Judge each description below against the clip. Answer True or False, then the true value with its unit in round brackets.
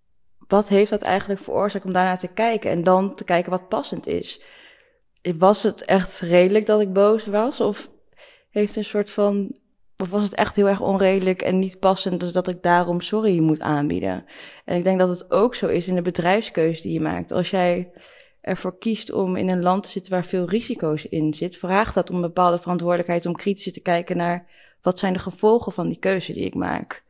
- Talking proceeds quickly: True (210 wpm)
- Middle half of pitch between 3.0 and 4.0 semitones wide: False (2.4 semitones)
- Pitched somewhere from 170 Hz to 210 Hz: True (185 Hz)